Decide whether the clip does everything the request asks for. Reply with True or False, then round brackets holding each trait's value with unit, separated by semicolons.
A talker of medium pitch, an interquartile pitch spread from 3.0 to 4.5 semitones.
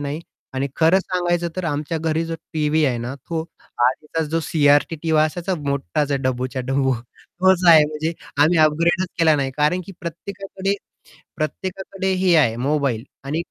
True (155 Hz; 3.5 semitones)